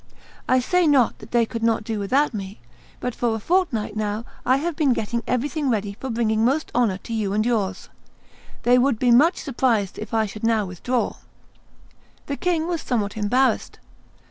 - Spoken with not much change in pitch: No, average, 3.8 semitones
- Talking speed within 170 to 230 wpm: Yes, average, 185 wpm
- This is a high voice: Yes, high, 235 Hz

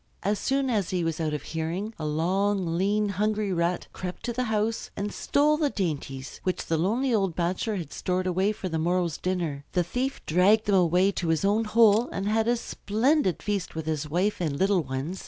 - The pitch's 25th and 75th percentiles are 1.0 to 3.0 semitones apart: No, average, 4.1 semitones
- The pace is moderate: No, fast, 210 wpm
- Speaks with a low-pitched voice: No, high, 190 Hz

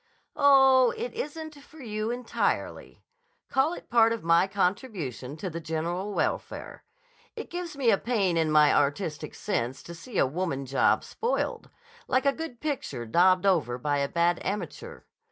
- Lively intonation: Yes, wide, 8.5 semitones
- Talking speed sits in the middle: Yes, average, 160 wpm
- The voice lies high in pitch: Yes, high, 195 Hz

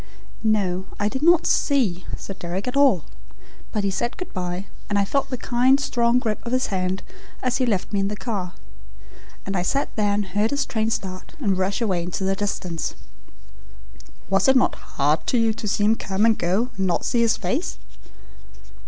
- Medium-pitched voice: No, high, 205 Hz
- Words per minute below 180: No, fast, 205 wpm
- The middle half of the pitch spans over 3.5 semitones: Yes, average, 4.2 semitones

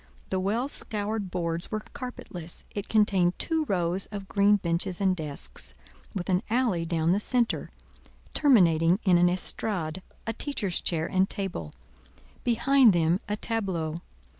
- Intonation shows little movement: No, average, 4.1 semitones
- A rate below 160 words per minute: Yes, average, 140 wpm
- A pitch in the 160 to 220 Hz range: Yes, high, 190 Hz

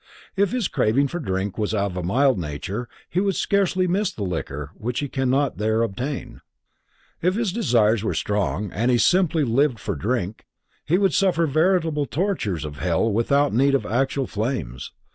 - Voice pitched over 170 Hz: No, low, 125 Hz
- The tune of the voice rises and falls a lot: Yes, wide, 8.2 semitones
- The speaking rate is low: No, average, 175 wpm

